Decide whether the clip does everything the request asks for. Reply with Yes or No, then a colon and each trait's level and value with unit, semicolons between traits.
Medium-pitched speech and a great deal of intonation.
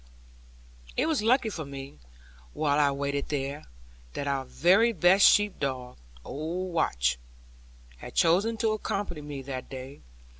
Yes: medium, 150 Hz; wide, 6.0 semitones